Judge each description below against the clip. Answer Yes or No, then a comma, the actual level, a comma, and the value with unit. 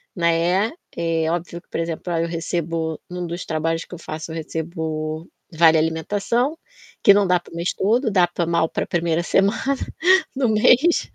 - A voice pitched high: No, medium, 170 Hz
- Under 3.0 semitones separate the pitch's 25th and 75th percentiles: Yes, narrow, 2.6 semitones